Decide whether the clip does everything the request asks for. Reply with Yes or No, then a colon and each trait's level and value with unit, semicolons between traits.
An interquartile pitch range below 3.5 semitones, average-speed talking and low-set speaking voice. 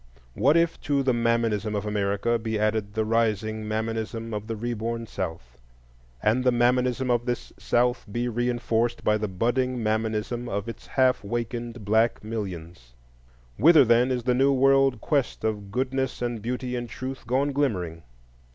Yes: narrow, 2.6 semitones; average, 160 wpm; low, 115 Hz